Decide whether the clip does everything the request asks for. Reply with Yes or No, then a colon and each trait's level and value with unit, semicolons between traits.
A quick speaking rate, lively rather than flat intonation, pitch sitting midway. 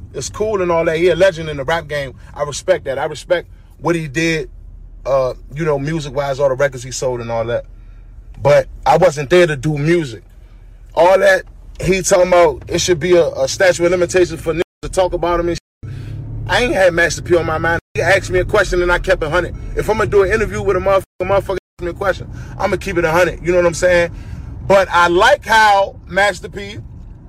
Yes: fast, 240 wpm; wide, 5.9 semitones; medium, 170 Hz